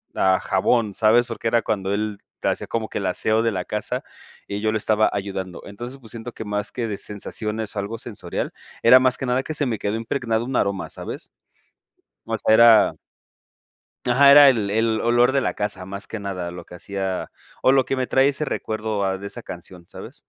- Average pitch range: Yes, average, 3.2 semitones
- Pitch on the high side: No, low, 110 Hz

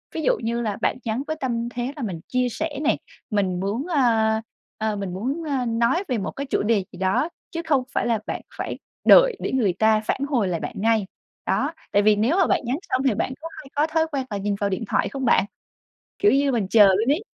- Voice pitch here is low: No, high, 235 Hz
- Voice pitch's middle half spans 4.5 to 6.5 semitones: Yes, average, 5.2 semitones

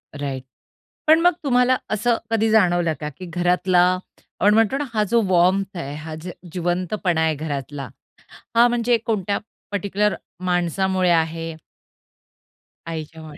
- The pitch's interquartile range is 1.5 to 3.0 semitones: No, average, 4.8 semitones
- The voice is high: No, medium, 180 Hz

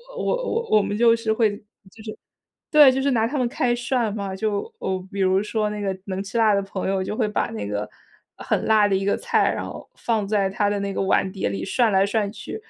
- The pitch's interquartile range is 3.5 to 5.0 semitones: No, average, 3.0 semitones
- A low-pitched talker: No, high, 210 Hz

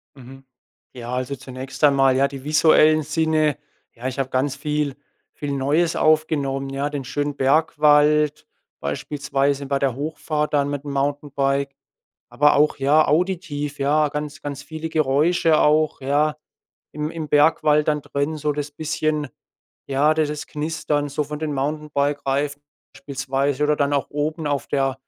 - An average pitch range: No, narrow, 1.7 semitones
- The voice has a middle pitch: Yes, medium, 145 Hz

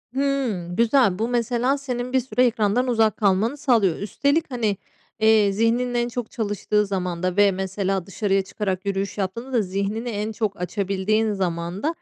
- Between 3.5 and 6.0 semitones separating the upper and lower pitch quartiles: Yes, average, 3.9 semitones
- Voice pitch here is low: No, high, 215 Hz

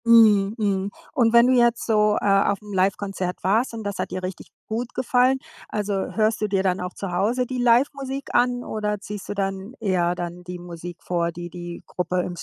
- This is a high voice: Yes, high, 205 Hz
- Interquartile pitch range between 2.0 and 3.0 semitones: No, average, 4.1 semitones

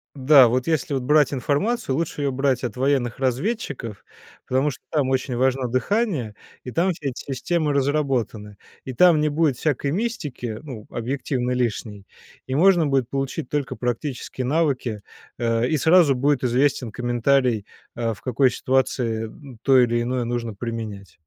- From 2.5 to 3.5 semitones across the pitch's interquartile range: Yes, average, 3.2 semitones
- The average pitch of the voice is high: No, low, 130 Hz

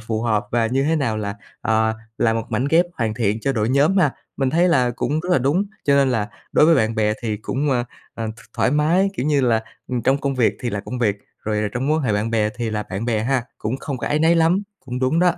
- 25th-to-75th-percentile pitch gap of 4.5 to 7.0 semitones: Yes, average, 4.8 semitones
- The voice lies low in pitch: Yes, low, 125 Hz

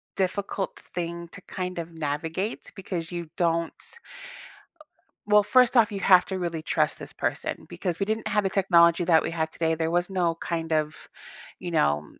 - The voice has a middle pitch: Yes, medium, 175 Hz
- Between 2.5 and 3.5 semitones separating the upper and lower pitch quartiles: Yes, average, 2.8 semitones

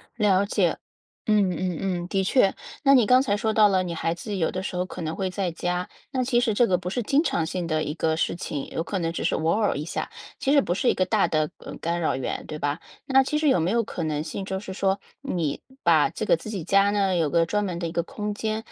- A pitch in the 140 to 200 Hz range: Yes, medium, 185 Hz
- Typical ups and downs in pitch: Yes, average, 4.1 semitones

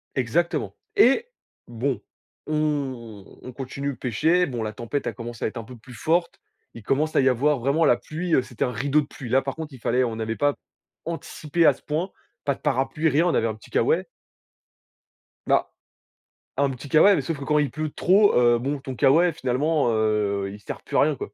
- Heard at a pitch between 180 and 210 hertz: No, low, 135 Hz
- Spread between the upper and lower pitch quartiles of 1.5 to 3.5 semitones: No, average, 4.5 semitones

